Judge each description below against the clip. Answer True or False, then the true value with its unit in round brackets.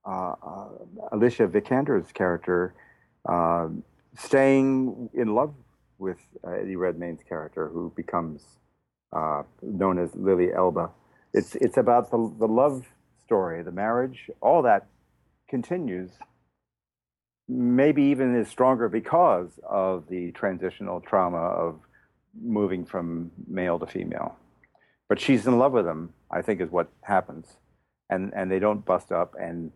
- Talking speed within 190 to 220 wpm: False (135 wpm)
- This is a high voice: False (95 Hz)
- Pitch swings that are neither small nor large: False (6.4 semitones)